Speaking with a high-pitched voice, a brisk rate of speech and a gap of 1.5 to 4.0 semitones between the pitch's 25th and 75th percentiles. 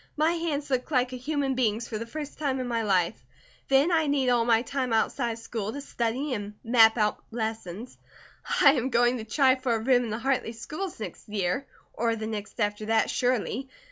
Yes: high, 240 Hz; fast, 210 wpm; average, 3.5 semitones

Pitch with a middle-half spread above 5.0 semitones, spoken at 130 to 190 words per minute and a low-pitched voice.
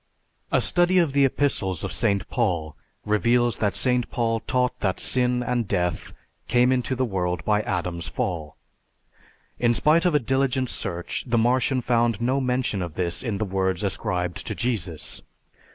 Yes: wide, 5.4 semitones; average, 165 wpm; low, 115 Hz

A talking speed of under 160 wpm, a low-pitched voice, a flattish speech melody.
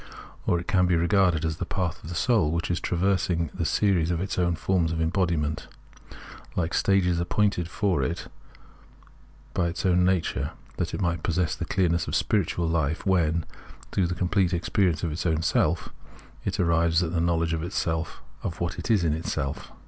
No: average, 185 wpm; very low, 85 Hz; narrow, 1.9 semitones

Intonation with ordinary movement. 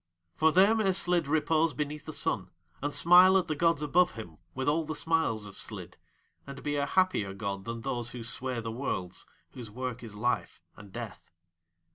No: wide, 6.1 semitones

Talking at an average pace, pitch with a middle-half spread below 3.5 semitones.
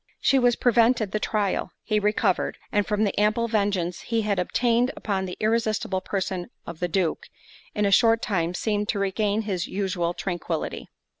Yes: average, 170 wpm; average, 2.8 semitones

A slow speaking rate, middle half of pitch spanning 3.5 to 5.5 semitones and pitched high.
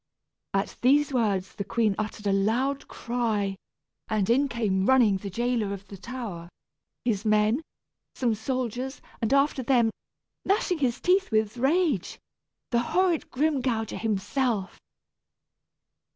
Yes: slow, 125 wpm; average, 4.1 semitones; high, 235 Hz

